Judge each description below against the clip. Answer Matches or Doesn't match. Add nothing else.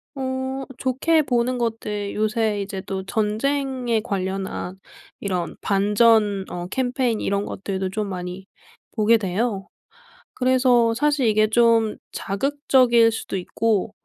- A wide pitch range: Doesn't match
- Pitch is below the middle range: Doesn't match